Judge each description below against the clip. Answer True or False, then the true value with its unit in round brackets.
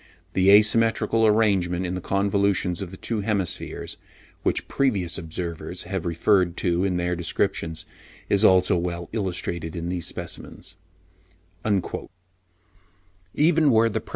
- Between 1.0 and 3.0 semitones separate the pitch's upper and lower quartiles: True (2.6 semitones)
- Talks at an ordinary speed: False (115 wpm)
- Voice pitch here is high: False (90 Hz)